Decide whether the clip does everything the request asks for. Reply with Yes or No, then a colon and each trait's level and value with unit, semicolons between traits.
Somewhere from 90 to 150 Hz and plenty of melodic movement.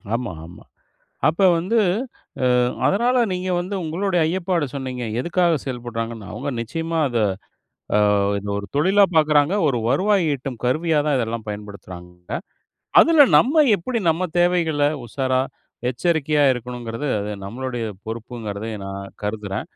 Yes: low, 135 Hz; wide, 7.1 semitones